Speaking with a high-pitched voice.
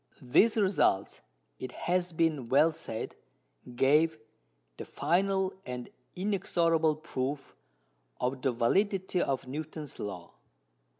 No: medium, 155 Hz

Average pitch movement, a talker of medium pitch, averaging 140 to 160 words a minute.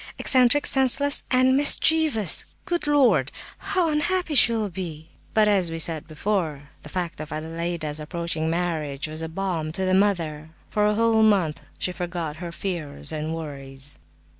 No: wide, 6.1 semitones; medium, 175 Hz; average, 155 wpm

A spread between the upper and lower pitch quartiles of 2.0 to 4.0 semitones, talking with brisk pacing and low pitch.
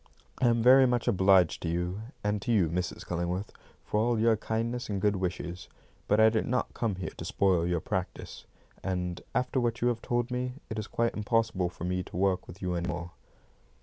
No: average, 4.5 semitones; fast, 210 wpm; low, 100 Hz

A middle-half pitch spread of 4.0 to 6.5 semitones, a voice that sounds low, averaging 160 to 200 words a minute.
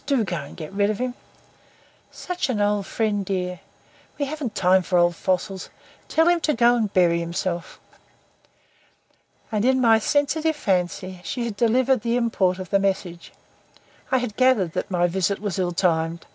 No: average, 5.2 semitones; high, 200 Hz; average, 175 wpm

